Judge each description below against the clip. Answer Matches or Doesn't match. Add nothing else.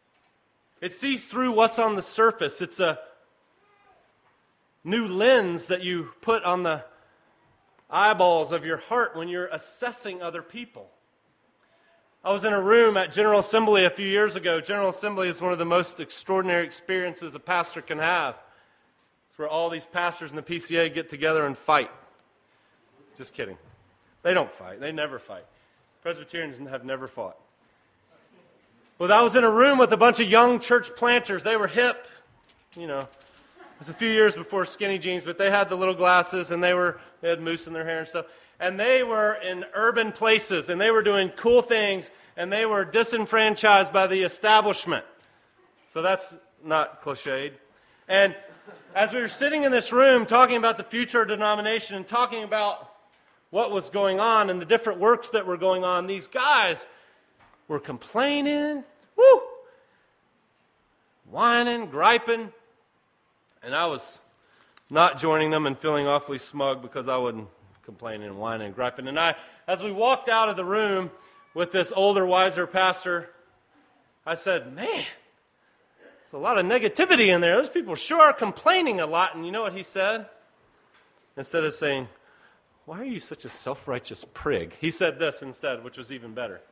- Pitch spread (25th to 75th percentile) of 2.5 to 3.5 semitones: Doesn't match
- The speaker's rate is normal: Matches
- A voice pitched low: Doesn't match